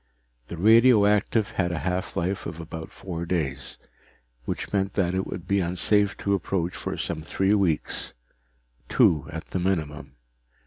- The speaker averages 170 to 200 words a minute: No, average, 150 wpm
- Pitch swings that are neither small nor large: Yes, average, 3.2 semitones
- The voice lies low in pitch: Yes, very low, 90 Hz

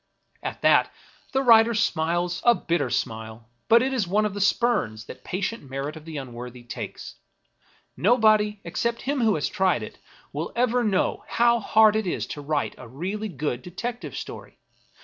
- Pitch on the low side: No, high, 190 Hz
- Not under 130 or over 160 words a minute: No, average, 175 wpm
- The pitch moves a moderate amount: No, wide, 7.7 semitones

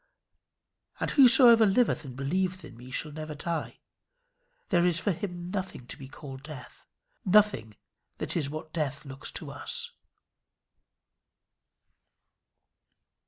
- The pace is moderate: No, slow, 120 wpm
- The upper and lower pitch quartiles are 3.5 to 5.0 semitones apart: No, wide, 5.6 semitones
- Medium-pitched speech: Yes, medium, 165 Hz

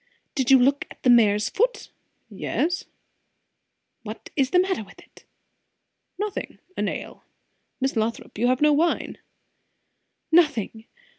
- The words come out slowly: Yes, slow, 130 wpm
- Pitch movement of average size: No, wide, 6.2 semitones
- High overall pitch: Yes, very high, 265 Hz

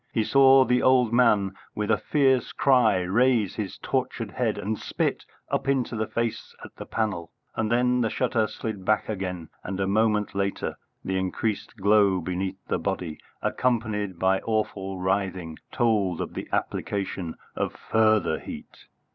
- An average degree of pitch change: Yes, average, 3.5 semitones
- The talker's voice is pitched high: No, low, 105 Hz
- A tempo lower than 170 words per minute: Yes, average, 155 wpm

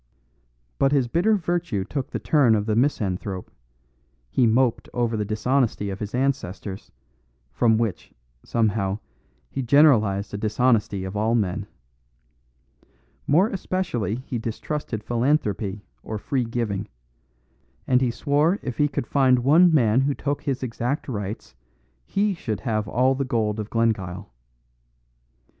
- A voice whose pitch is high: No, low, 115 Hz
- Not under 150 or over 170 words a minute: No, slow, 135 wpm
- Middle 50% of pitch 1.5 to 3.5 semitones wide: No, average, 4.6 semitones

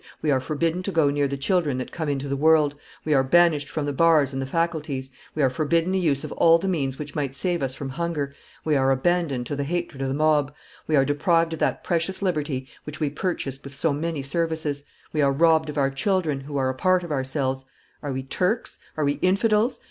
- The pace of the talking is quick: Yes, fast, 235 wpm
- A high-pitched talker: No, medium, 150 Hz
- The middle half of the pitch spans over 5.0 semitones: No, average, 3.4 semitones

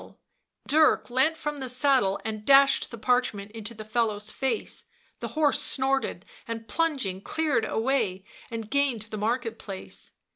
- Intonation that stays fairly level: No, average, 4.1 semitones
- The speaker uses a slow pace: No, average, 175 wpm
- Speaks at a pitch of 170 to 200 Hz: No, high, 235 Hz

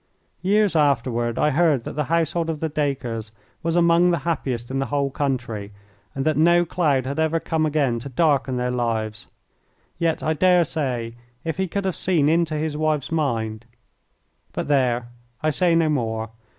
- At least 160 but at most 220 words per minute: Yes, average, 175 wpm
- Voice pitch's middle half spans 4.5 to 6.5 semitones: Yes, average, 4.8 semitones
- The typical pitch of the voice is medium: Yes, medium, 150 Hz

